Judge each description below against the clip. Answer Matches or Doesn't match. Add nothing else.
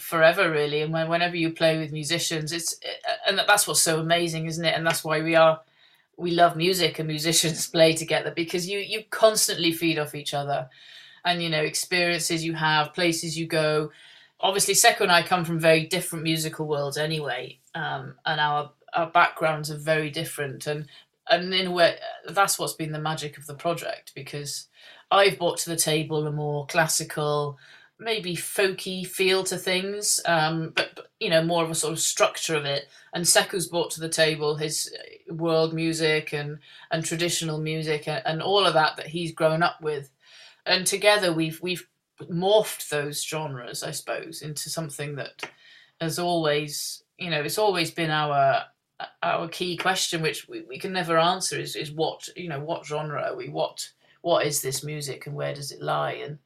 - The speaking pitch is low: Doesn't match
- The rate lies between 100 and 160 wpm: Doesn't match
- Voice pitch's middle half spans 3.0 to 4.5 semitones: Doesn't match